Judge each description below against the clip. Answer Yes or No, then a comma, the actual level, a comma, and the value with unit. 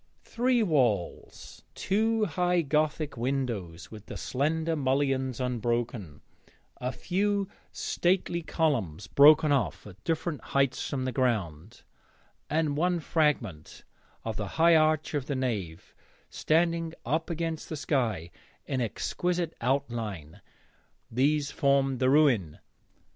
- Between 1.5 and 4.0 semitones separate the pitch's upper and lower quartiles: No, wide, 5.5 semitones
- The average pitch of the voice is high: No, medium, 140 Hz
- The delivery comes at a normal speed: No, slow, 115 wpm